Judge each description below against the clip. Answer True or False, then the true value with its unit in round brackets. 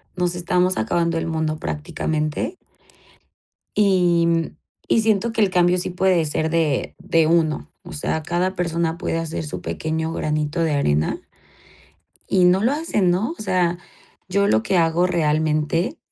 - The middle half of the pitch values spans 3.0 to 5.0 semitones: False (2.5 semitones)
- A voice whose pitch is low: False (170 Hz)